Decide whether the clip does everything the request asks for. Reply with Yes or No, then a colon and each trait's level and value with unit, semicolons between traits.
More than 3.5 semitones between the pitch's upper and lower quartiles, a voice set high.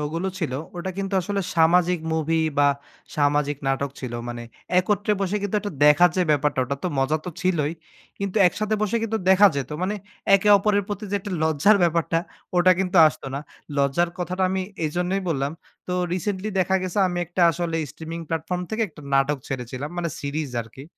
No: average, 4.5 semitones; medium, 175 Hz